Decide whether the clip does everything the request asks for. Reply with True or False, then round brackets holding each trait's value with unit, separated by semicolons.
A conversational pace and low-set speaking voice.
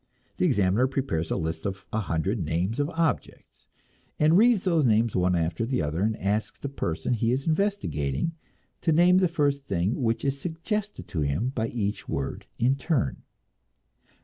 True (170 wpm; 120 Hz)